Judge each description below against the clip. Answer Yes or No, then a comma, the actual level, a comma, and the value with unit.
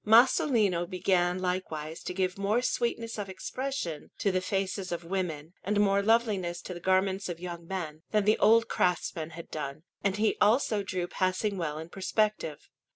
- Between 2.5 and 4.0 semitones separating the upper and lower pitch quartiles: Yes, average, 3.2 semitones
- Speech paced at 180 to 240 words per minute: No, average, 170 wpm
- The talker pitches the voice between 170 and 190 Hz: Yes, medium, 185 Hz